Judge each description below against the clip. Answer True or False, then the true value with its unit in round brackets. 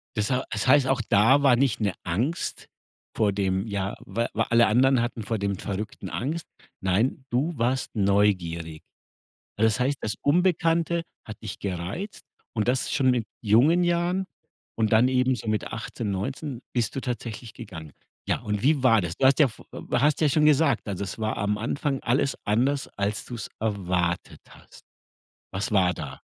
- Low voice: True (115 Hz)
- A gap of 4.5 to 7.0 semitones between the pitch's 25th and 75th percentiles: True (4.9 semitones)